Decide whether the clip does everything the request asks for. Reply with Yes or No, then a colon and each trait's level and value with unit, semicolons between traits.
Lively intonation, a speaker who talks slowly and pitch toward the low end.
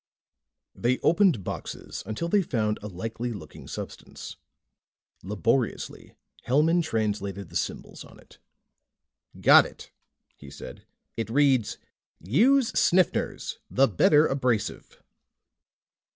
Yes: wide, 6.6 semitones; slow, 105 wpm; low, 120 Hz